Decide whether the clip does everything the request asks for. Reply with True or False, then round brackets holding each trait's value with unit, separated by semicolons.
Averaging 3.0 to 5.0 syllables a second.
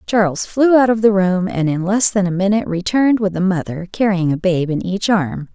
False (5.4 syllables/s)